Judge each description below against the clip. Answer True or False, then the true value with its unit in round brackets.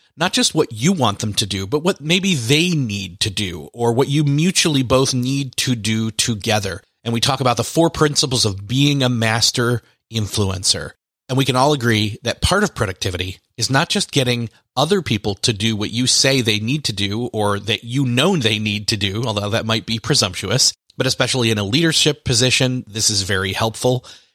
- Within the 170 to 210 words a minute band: True (205 wpm)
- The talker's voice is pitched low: True (120 Hz)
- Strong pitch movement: False (4.1 semitones)